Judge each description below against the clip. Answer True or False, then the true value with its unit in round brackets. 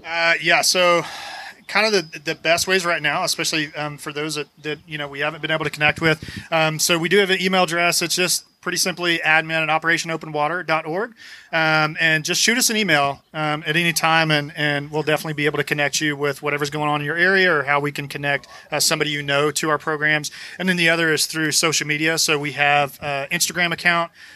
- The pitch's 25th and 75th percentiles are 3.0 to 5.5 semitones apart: False (2.4 semitones)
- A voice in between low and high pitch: True (155 Hz)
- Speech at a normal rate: False (230 wpm)